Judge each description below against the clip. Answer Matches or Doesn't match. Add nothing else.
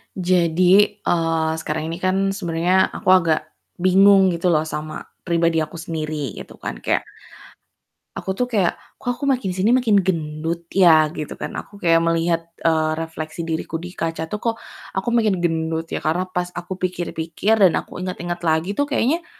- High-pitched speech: Doesn't match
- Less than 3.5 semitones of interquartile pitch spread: Matches